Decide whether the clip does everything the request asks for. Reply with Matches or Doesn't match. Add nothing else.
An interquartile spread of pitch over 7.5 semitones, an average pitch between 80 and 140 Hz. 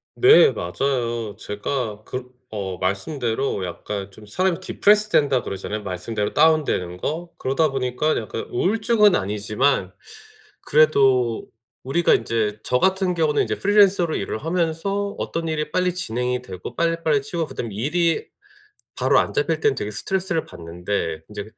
Matches